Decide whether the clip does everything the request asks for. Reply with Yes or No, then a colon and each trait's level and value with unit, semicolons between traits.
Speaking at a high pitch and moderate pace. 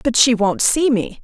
No: high, 240 Hz; fast, 245 wpm